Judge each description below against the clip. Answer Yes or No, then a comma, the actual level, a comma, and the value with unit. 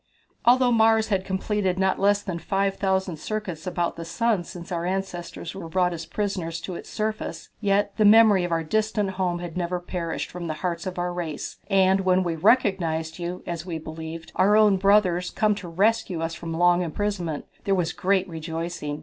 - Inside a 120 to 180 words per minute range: No, average, 190 wpm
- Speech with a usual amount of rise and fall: Yes, average, 3.0 semitones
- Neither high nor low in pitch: Yes, medium, 180 Hz